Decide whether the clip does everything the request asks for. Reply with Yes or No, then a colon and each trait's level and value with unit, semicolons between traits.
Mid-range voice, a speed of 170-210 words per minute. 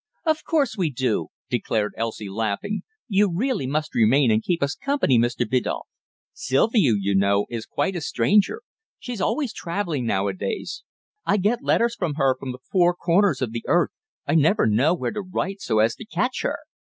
Yes: medium, 155 Hz; average, 190 wpm